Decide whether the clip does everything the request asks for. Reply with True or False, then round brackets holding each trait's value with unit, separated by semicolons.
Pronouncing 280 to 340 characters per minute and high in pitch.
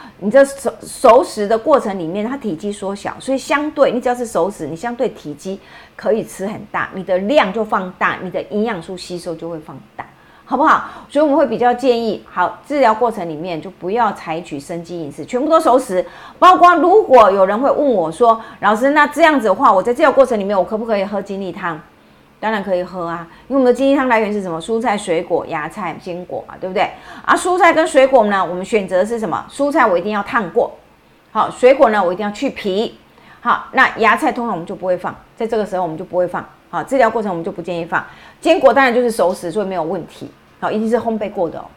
False (350 characters per minute; 210 Hz)